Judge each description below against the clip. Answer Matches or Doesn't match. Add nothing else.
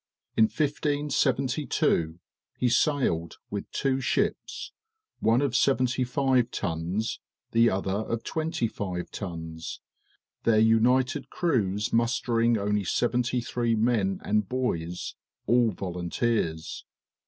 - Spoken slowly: Matches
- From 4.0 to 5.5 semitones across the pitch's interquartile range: Matches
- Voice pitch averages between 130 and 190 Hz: Doesn't match